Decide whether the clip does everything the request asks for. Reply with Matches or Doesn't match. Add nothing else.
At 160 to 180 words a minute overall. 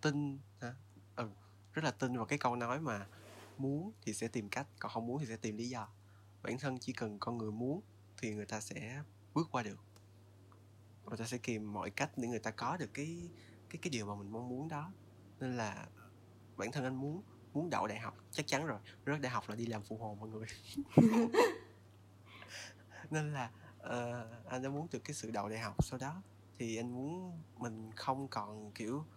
Doesn't match